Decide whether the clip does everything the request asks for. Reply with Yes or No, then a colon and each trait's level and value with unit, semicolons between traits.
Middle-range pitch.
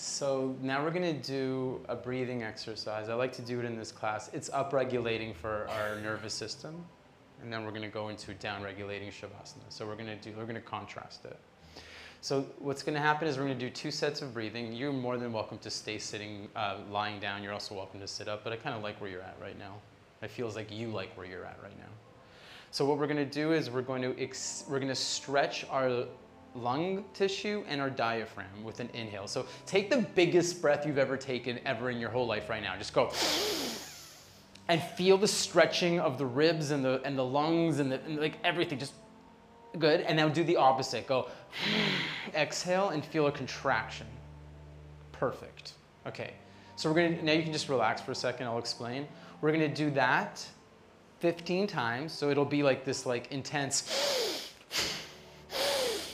No: low, 130 Hz